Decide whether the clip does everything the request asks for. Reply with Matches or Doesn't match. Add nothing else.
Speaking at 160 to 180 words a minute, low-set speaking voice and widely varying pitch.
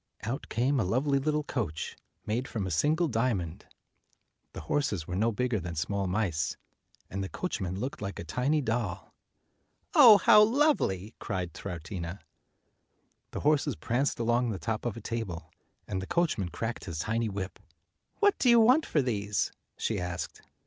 Matches